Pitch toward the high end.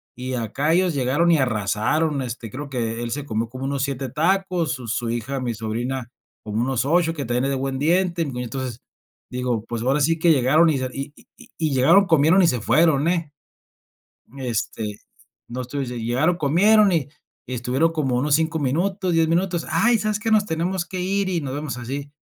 No: medium, 140 Hz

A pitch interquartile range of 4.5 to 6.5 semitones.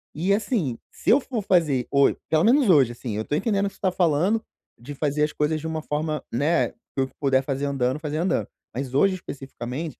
Yes: average, 5.3 semitones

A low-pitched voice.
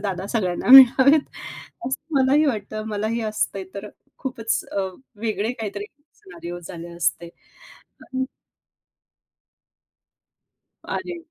No: high, 220 Hz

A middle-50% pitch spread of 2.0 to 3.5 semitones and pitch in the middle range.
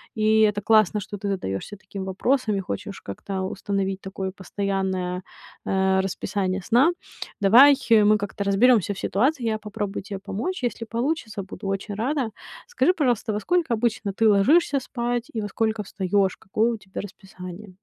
No: average, 3.1 semitones; high, 205 Hz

